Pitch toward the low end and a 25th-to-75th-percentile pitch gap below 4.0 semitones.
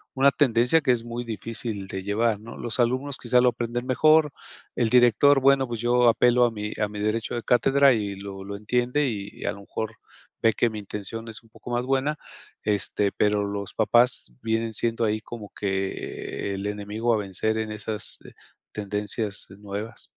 Yes: low, 115 Hz; average, 2.8 semitones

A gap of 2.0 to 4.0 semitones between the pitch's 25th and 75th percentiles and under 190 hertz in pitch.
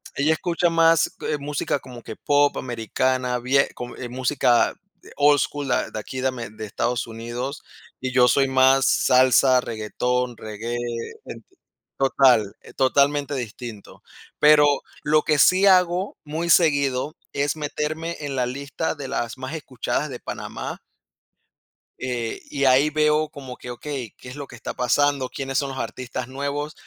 Yes: average, 2.9 semitones; low, 135 Hz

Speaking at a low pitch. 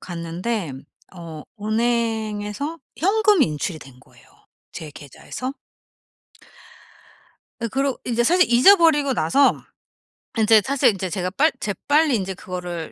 No: high, 220 Hz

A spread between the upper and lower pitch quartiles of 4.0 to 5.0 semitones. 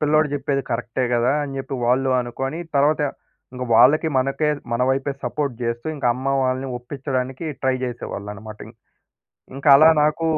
No: average, 2.7 semitones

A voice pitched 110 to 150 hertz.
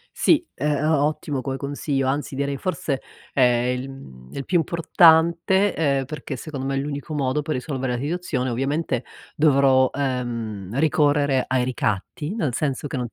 Yes: medium, 140 Hz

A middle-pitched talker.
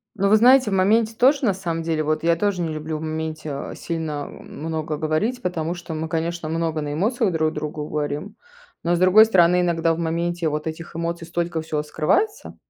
Yes: medium, 165 Hz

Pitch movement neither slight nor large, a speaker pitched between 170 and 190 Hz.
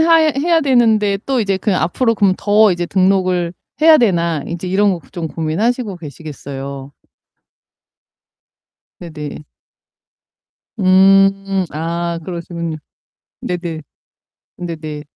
Yes: average, 3.7 semitones; medium, 185 Hz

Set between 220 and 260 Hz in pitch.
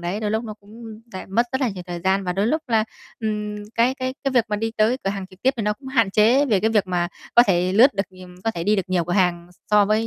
No: high, 210 Hz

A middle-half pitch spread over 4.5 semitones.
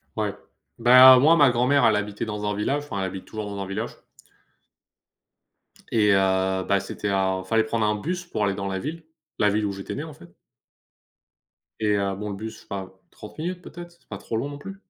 Yes: wide, 5.5 semitones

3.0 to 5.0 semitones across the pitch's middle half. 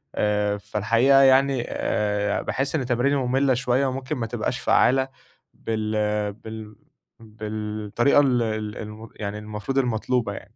Yes: average, 3.7 semitones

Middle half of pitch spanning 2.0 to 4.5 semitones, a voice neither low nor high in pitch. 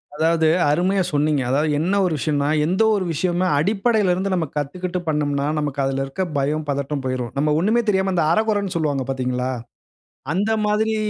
No: average, 5.0 semitones; medium, 160 Hz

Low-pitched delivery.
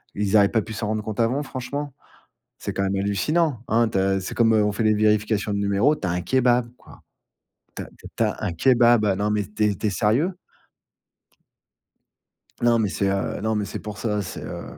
Yes: low, 105 Hz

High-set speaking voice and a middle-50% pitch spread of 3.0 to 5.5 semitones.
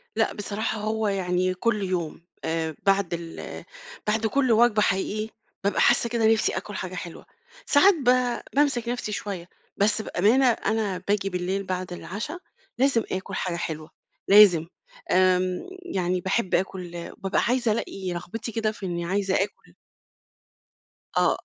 Yes: high, 200 Hz; average, 3.5 semitones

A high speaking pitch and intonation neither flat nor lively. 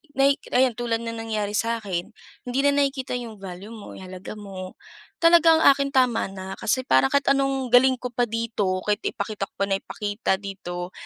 Yes: high, 225 Hz; average, 4.9 semitones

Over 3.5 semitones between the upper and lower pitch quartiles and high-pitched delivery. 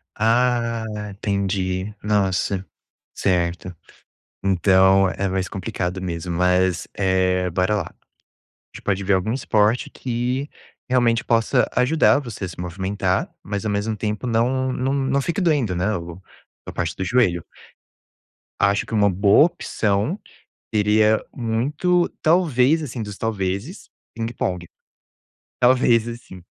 No: average, 4.6 semitones; low, 105 Hz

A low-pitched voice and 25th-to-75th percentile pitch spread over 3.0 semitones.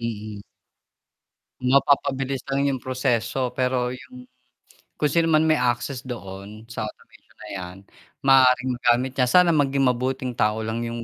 No: low, 125 Hz; average, 2.7 semitones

